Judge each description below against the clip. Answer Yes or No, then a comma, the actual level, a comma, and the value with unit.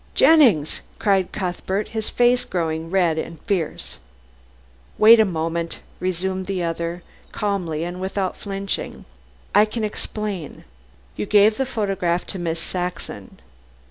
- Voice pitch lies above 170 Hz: Yes, medium, 185 Hz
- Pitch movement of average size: Yes, average, 3.6 semitones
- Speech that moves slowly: Yes, slow, 125 wpm